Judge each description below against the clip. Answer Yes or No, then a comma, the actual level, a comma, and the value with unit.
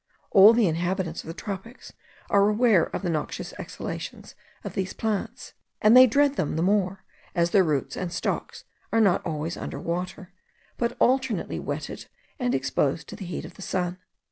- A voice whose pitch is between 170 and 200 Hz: Yes, high, 190 Hz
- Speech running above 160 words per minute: Yes, average, 175 wpm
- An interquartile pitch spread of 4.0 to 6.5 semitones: Yes, average, 4.4 semitones